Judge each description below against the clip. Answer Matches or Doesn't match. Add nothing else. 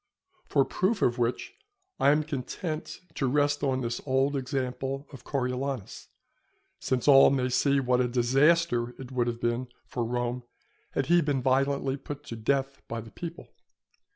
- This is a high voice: Doesn't match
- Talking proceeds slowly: Doesn't match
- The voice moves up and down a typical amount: Doesn't match